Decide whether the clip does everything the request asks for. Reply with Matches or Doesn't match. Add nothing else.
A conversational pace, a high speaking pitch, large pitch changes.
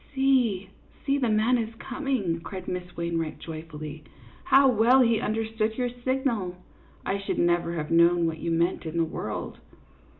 Matches